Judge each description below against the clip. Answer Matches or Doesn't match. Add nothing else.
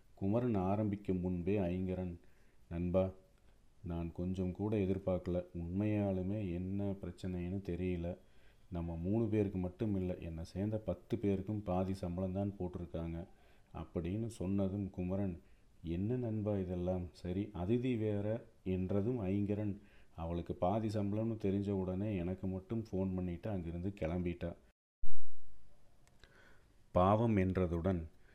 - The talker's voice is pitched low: Matches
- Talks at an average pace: Matches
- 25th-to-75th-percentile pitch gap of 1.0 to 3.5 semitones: Matches